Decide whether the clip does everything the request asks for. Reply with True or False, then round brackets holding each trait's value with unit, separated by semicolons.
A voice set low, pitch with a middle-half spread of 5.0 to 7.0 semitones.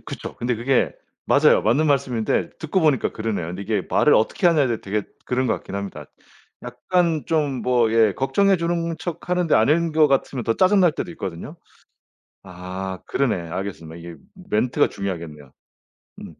False (125 Hz; 8.1 semitones)